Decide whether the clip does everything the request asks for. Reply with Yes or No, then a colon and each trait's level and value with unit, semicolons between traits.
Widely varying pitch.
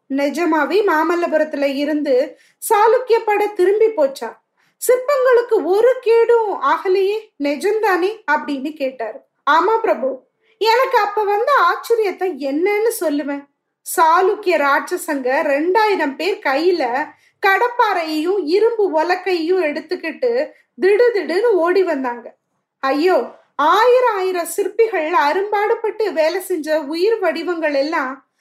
Yes: wide, 5.9 semitones